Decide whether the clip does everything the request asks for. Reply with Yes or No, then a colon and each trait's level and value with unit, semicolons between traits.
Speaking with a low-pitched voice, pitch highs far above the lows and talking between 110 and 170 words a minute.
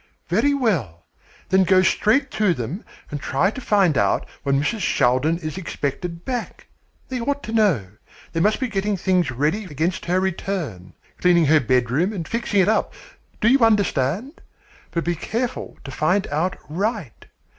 No: medium, 180 Hz; wide, 6.3 semitones; average, 165 wpm